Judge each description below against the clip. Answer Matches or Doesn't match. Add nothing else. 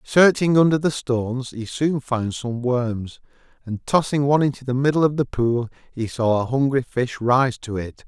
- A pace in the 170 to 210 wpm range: Matches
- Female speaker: Doesn't match